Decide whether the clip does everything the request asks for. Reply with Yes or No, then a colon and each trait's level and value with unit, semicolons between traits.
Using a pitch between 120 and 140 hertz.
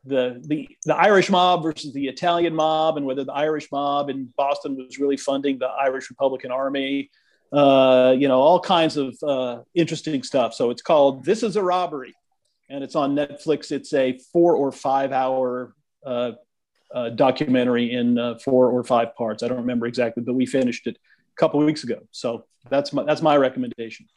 Yes: low, 135 Hz